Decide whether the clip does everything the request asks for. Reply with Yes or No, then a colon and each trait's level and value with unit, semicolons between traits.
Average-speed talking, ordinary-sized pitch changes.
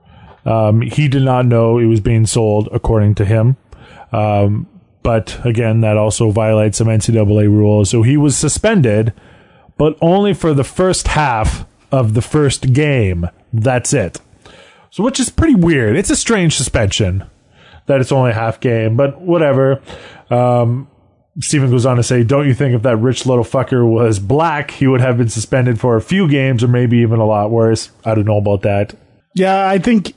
Yes: average, 185 wpm; average, 4.1 semitones